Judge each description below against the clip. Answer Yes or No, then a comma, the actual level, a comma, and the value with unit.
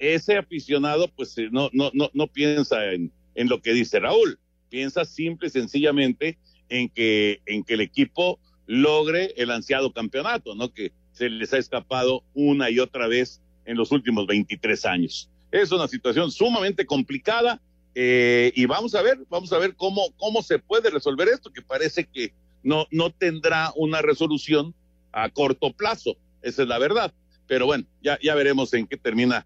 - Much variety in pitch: Yes, wide, 6.2 semitones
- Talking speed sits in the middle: Yes, average, 175 wpm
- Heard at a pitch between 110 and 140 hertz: Yes, low, 135 Hz